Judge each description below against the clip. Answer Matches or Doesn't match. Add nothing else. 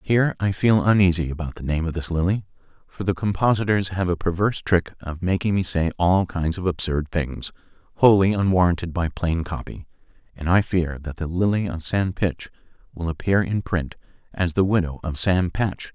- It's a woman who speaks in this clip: Doesn't match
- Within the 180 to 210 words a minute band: Matches